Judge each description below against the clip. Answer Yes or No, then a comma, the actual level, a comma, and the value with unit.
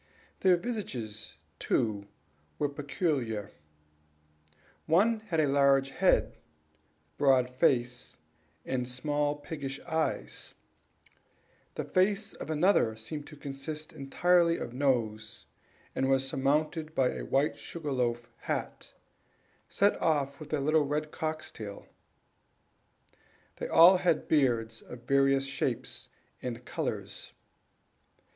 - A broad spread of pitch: No, average, 3.8 semitones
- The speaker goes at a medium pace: No, slow, 110 wpm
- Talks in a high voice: No, medium, 140 Hz